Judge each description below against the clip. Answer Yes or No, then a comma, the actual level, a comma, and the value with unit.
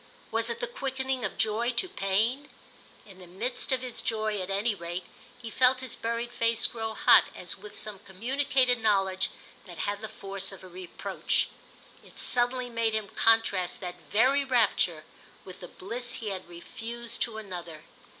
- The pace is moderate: Yes, average, 170 wpm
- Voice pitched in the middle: No, high, 220 Hz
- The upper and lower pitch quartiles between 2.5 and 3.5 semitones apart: No, average, 4.3 semitones